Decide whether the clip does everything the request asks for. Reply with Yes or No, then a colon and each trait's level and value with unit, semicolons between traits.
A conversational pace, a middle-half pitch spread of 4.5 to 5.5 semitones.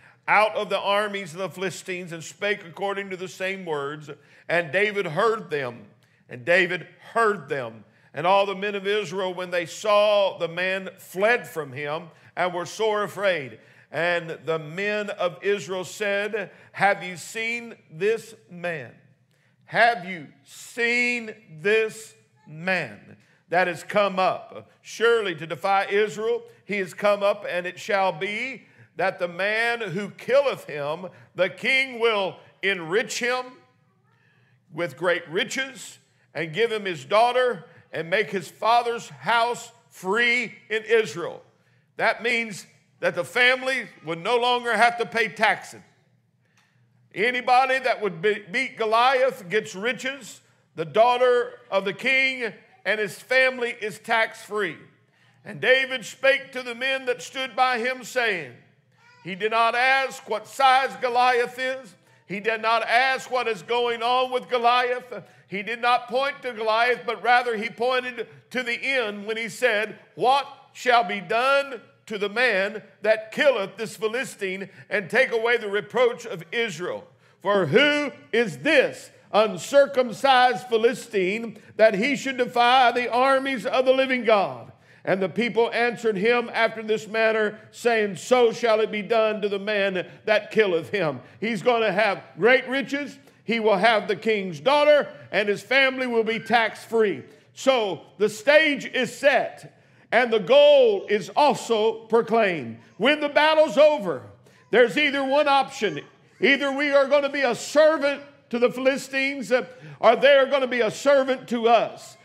Yes: average, 150 wpm; average, 4.8 semitones